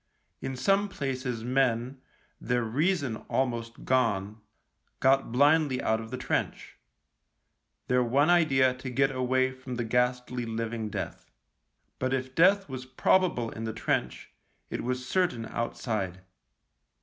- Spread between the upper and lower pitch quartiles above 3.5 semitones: No, narrow, 2.5 semitones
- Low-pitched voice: Yes, low, 125 Hz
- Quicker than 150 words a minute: No, slow, 135 wpm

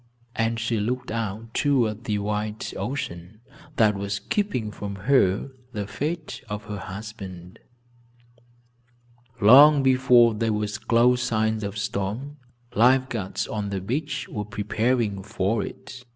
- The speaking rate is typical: No, slow, 130 wpm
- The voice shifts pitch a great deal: No, average, 3.4 semitones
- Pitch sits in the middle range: No, low, 110 Hz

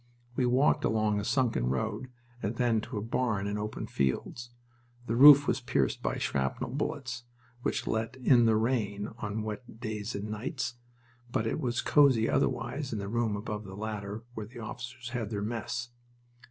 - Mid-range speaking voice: No, low, 115 Hz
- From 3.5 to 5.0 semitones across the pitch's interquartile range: No, average, 2.8 semitones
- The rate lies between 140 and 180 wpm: Yes, average, 175 wpm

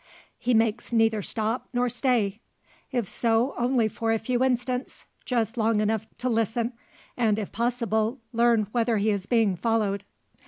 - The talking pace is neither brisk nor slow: Yes, average, 155 wpm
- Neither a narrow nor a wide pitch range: No, narrow, 1.9 semitones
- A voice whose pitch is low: No, high, 225 Hz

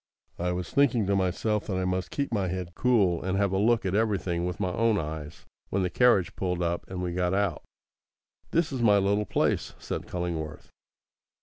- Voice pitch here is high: No, very low, 95 Hz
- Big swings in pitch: No, average, 3.0 semitones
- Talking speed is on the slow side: No, average, 200 wpm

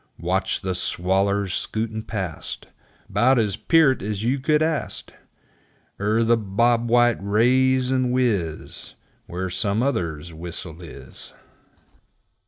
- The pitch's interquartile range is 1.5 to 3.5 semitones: No, average, 4.9 semitones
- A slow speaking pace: Yes, slow, 115 wpm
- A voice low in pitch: Yes, low, 110 Hz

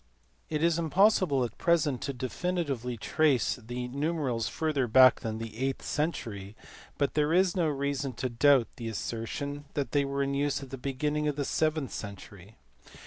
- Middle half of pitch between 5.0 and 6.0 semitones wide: No, average, 3.7 semitones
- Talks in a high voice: No, medium, 140 Hz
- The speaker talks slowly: No, average, 170 wpm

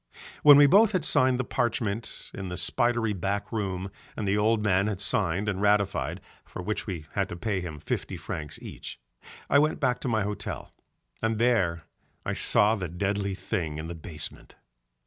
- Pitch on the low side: Yes, low, 105 Hz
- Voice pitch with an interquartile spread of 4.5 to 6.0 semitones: No, average, 3.9 semitones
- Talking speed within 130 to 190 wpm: Yes, average, 185 wpm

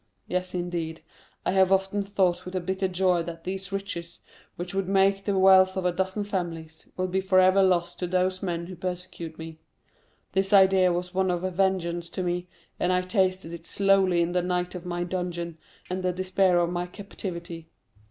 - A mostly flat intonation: Yes, narrow, 1.6 semitones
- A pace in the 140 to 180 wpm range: No, average, 190 wpm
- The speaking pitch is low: No, medium, 180 Hz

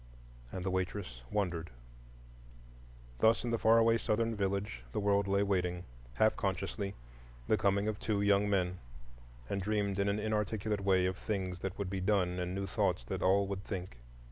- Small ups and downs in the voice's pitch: Yes, narrow, 2.1 semitones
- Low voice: Yes, low, 100 Hz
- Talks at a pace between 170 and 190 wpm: Yes, average, 180 wpm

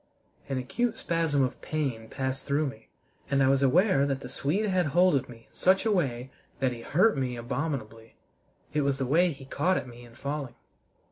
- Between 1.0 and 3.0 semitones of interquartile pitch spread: No, average, 4.5 semitones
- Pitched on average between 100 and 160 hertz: Yes, medium, 140 Hz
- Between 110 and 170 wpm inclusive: No, fast, 205 wpm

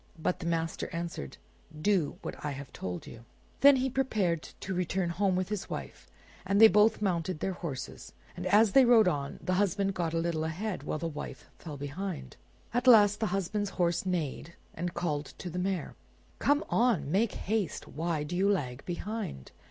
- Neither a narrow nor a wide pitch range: Yes, average, 4.1 semitones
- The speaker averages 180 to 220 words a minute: Yes, average, 185 wpm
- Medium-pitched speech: Yes, medium, 180 Hz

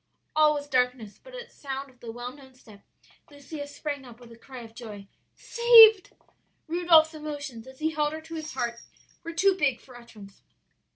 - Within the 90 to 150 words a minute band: No, average, 185 wpm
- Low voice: No, very high, 285 Hz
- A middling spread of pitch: Yes, average, 4.6 semitones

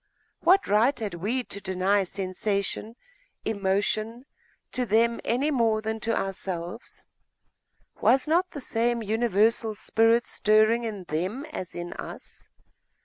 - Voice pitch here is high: Yes, high, 220 Hz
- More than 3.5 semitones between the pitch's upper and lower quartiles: No, average, 3.1 semitones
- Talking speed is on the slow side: Yes, slow, 125 wpm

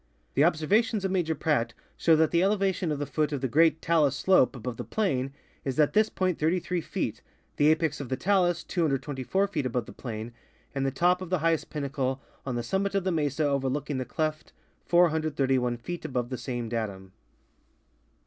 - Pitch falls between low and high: Yes, medium, 150 Hz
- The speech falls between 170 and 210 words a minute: Yes, average, 190 wpm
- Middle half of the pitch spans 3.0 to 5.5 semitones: Yes, average, 5.0 semitones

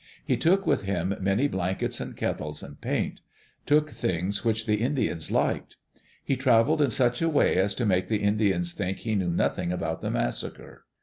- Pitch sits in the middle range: No, low, 100 Hz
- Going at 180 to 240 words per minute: Yes, average, 190 wpm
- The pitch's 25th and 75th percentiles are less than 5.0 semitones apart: No, wide, 5.4 semitones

